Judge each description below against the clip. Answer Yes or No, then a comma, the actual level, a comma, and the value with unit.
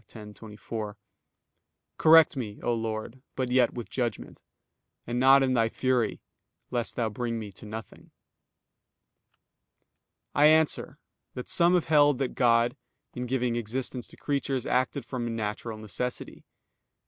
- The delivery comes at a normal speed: No, slow, 130 wpm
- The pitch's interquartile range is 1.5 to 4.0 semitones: Yes, average, 2.8 semitones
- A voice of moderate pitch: No, low, 120 Hz